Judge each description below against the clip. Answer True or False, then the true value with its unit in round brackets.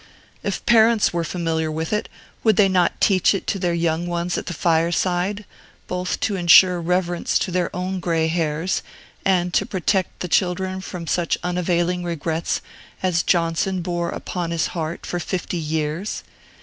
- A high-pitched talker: False (175 Hz)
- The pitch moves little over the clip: True (1.8 semitones)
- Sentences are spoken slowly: False (160 wpm)